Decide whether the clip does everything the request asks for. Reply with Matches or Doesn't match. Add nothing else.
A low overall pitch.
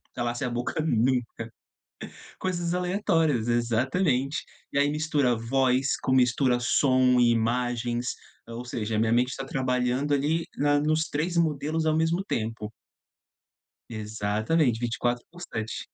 Matches